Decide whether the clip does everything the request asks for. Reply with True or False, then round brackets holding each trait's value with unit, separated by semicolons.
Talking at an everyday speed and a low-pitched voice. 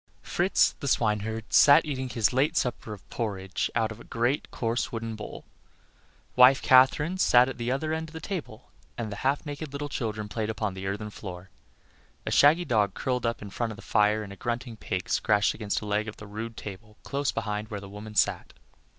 False (210 wpm; 115 Hz)